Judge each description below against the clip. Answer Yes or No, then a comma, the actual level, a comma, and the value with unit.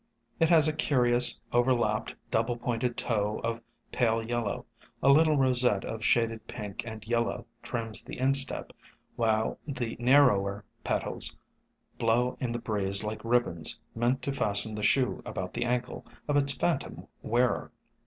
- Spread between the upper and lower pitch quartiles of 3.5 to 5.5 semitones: No, narrow, 2.5 semitones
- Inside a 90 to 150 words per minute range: Yes, average, 145 wpm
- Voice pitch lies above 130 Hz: No, low, 120 Hz